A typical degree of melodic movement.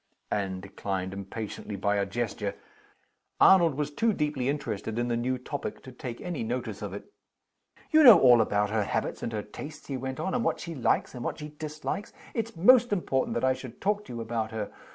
No: wide, 6.4 semitones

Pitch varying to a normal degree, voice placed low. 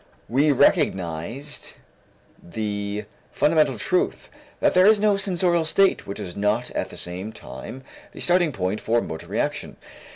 No: wide, 9.0 semitones; low, 125 Hz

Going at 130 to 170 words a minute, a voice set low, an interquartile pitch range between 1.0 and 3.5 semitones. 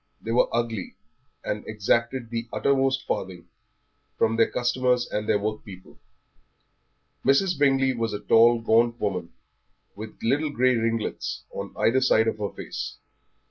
Yes: average, 140 wpm; low, 115 Hz; average, 3.0 semitones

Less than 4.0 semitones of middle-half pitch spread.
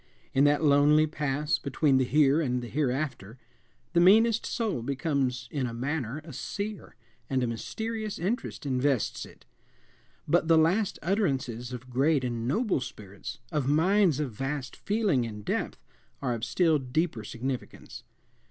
No: average, 4.6 semitones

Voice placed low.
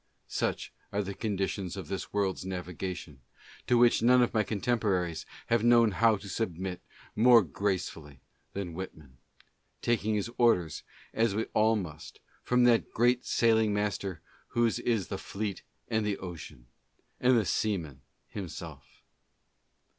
Yes: low, 100 Hz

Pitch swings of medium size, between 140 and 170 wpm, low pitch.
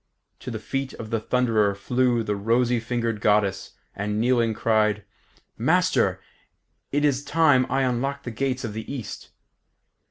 Yes: average, 3.1 semitones; average, 150 wpm; low, 120 Hz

